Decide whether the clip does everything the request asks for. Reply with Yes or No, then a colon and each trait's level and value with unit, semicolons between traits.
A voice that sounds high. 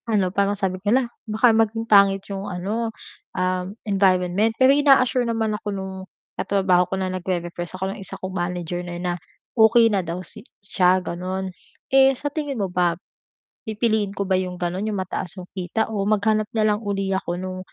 Yes: high, 195 Hz